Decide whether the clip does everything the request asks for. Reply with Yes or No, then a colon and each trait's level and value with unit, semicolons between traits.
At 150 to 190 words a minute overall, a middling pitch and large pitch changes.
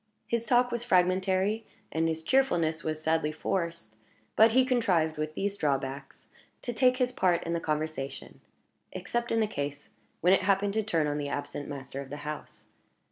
Yes: average, 180 wpm; medium, 170 Hz; wide, 6.3 semitones